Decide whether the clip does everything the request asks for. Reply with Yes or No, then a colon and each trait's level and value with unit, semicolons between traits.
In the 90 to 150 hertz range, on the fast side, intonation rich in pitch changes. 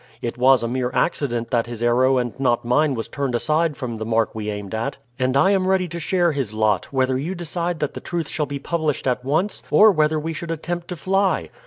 Yes: medium, 140 Hz; fast, 235 wpm; wide, 5.9 semitones